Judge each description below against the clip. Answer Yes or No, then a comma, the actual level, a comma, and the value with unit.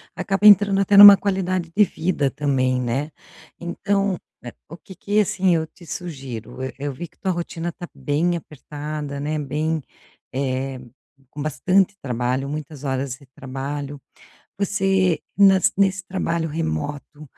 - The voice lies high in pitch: No, medium, 155 Hz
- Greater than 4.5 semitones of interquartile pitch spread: Yes, wide, 5.4 semitones